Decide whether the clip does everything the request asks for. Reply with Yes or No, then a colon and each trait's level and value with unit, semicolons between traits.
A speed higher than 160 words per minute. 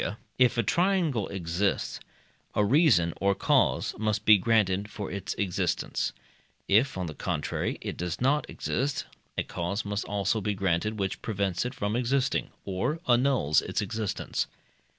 No: average, 150 wpm